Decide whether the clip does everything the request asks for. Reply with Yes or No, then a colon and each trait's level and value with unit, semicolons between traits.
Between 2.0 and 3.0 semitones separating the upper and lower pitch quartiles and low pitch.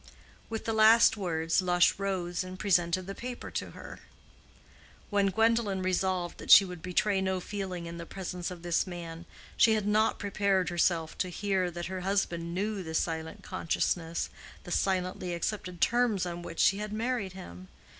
No: average, 2.7 semitones; medium, 185 Hz